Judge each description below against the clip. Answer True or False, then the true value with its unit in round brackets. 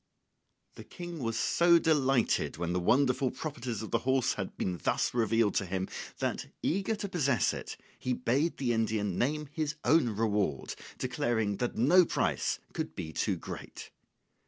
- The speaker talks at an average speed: True (165 wpm)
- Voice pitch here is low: True (125 Hz)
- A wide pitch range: True (6.2 semitones)